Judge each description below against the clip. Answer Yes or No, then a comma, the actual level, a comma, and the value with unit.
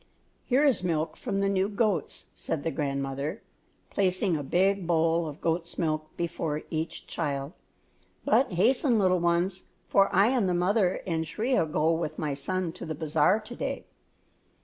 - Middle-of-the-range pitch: Yes, medium, 175 Hz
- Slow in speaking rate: No, average, 165 wpm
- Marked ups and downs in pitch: No, average, 3.9 semitones